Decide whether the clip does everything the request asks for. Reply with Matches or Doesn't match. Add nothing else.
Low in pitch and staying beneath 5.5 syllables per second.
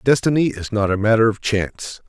Doesn't match